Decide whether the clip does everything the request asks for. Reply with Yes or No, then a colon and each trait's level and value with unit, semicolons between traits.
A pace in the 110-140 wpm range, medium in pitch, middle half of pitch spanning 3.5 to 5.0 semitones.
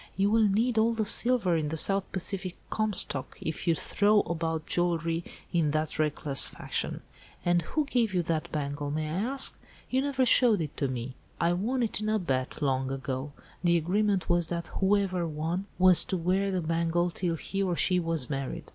No: average, 190 wpm; medium, 175 Hz; average, 4.4 semitones